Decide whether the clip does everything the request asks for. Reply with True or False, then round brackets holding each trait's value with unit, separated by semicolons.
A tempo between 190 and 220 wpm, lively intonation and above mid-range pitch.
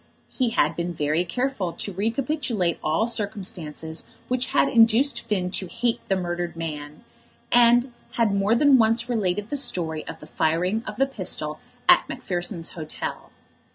False (155 wpm; 5.7 semitones; 200 Hz)